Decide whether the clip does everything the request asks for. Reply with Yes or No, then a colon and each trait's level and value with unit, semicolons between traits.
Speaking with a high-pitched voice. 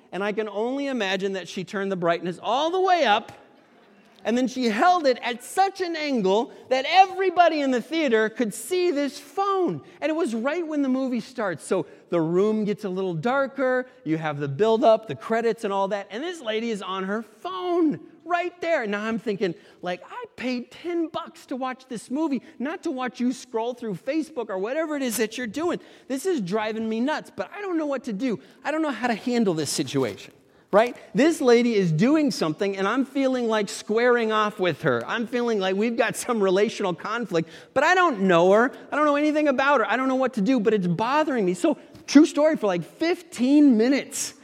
Yes: high, 245 Hz